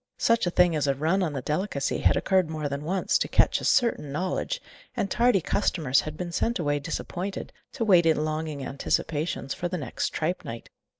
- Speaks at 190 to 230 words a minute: Yes, average, 195 wpm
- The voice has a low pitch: No, medium, 160 Hz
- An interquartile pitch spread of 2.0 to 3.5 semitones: No, average, 4.3 semitones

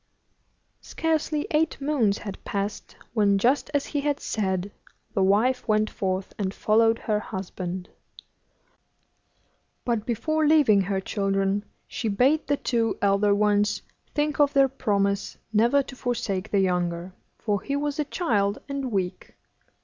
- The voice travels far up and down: Yes, wide, 5.7 semitones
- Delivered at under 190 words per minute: Yes, average, 140 wpm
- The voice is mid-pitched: No, high, 215 Hz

